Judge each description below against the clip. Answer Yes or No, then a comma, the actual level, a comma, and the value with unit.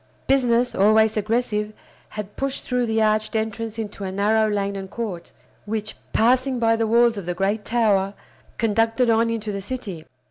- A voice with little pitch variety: Yes, narrow, 2.1 semitones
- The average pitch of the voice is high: Yes, high, 220 Hz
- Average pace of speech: Yes, average, 170 wpm